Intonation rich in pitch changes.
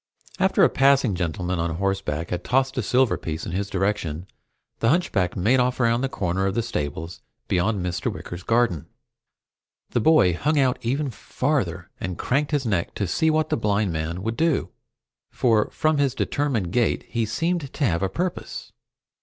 Yes: wide, 6.7 semitones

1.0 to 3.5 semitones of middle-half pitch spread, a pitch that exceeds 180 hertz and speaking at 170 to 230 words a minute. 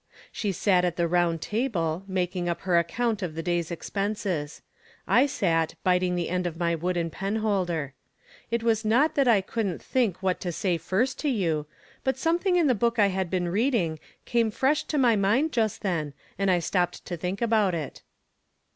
No: average, 4.8 semitones; high, 190 Hz; average, 190 wpm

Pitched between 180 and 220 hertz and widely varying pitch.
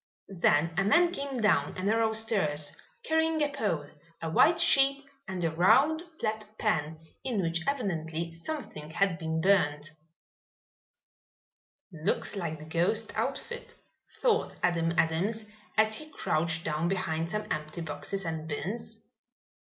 Yes: medium, 185 Hz; wide, 5.8 semitones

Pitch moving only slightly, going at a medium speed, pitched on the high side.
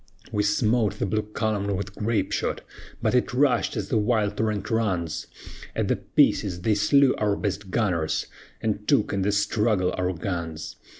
No: narrow, 2.3 semitones; average, 170 wpm; low, 105 Hz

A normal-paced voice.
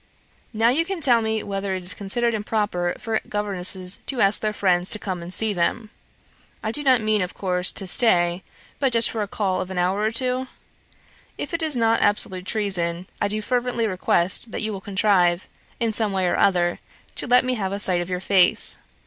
No: fast, 210 wpm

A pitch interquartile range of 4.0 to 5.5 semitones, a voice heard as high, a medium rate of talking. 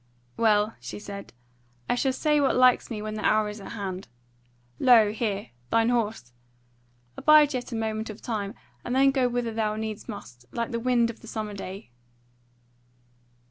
No: average, 2.7 semitones; high, 225 Hz; average, 175 wpm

